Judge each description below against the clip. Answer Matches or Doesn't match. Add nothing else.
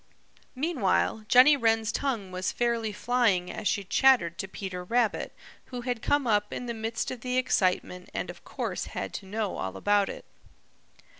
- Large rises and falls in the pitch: Doesn't match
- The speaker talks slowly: Doesn't match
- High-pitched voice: Matches